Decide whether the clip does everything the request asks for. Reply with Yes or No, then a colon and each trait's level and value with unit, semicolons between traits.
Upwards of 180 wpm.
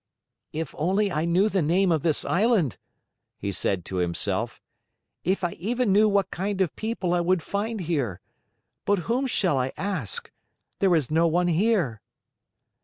No: average, 165 wpm